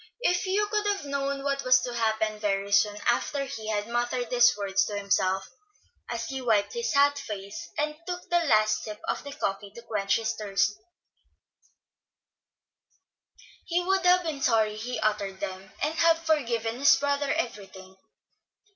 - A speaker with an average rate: Yes, average, 165 wpm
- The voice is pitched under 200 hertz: No, high, 235 Hz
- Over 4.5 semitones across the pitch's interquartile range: Yes, wide, 5.5 semitones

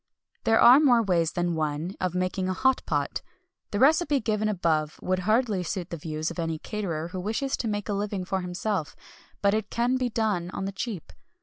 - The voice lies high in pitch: Yes, high, 195 Hz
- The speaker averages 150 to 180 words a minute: No, fast, 205 wpm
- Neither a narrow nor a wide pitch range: Yes, average, 4.1 semitones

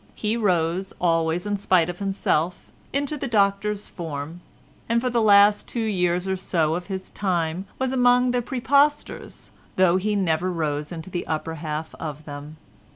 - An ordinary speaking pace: Yes, average, 165 wpm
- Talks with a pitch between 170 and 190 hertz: Yes, medium, 185 Hz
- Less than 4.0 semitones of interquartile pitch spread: No, average, 4.5 semitones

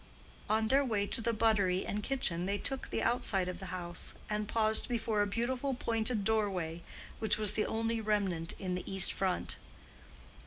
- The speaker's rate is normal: Yes, average, 185 wpm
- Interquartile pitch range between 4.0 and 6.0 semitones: No, average, 3.1 semitones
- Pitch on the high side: Yes, high, 210 Hz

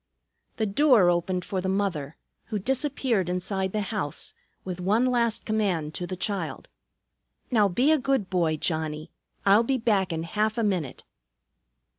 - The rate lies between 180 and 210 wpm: No, average, 155 wpm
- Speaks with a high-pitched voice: Yes, high, 195 Hz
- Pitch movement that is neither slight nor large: Yes, average, 4.2 semitones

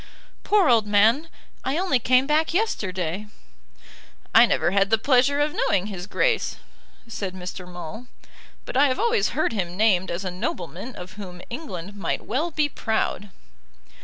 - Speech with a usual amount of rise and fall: No, wide, 7.2 semitones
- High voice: Yes, high, 220 Hz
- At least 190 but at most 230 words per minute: No, average, 160 wpm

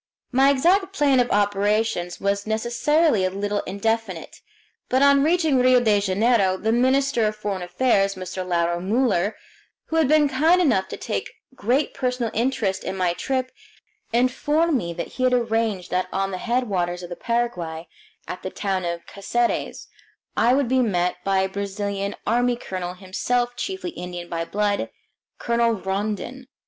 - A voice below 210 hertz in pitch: No, high, 220 Hz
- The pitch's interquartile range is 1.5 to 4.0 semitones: No, average, 5.1 semitones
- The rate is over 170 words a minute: No, average, 160 wpm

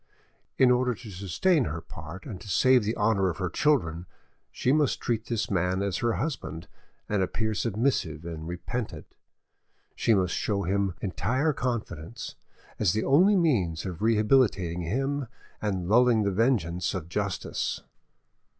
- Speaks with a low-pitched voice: Yes, low, 105 Hz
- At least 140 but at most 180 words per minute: Yes, average, 150 wpm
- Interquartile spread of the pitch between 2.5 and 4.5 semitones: No, wide, 5.5 semitones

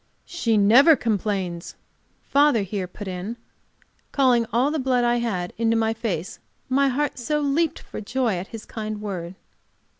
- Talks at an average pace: Yes, average, 155 wpm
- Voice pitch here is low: No, high, 230 Hz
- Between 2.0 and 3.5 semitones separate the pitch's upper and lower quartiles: No, average, 4.6 semitones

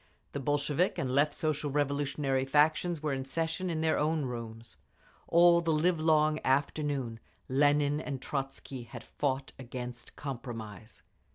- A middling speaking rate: No, slow, 130 wpm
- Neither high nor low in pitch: Yes, medium, 145 Hz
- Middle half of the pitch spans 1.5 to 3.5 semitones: Yes, average, 2.8 semitones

